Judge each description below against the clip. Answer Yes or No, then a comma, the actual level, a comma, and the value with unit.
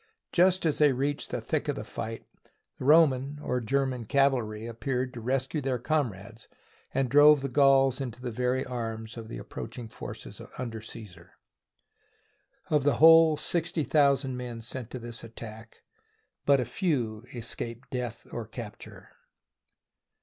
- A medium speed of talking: Yes, average, 150 wpm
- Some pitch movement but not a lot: Yes, average, 3.4 semitones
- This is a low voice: Yes, low, 125 Hz